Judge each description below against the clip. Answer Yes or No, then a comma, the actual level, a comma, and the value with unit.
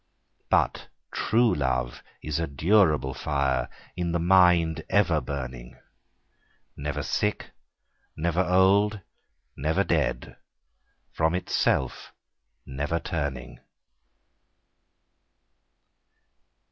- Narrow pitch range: No, average, 4.7 semitones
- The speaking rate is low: Yes, slow, 80 wpm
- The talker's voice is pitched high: No, very low, 80 Hz